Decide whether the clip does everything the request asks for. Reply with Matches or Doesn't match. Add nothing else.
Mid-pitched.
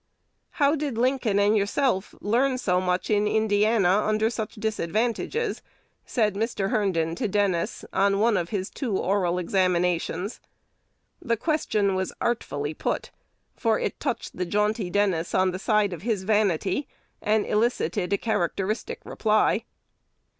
Doesn't match